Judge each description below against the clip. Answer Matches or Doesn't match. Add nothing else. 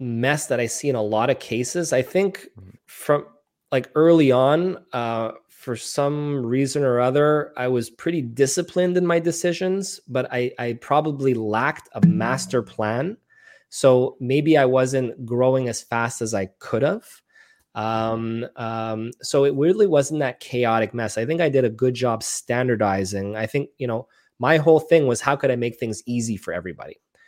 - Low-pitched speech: Matches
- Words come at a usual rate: Matches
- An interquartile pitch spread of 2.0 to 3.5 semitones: Doesn't match